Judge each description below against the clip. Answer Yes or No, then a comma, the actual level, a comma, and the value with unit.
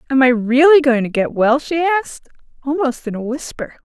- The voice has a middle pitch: No, very high, 265 Hz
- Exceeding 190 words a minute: Yes, average, 200 wpm